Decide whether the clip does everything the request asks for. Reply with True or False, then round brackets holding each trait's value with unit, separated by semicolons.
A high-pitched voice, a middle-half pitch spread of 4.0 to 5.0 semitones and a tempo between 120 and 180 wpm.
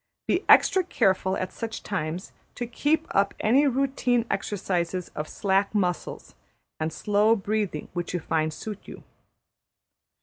True (200 Hz; 4.5 semitones; 135 wpm)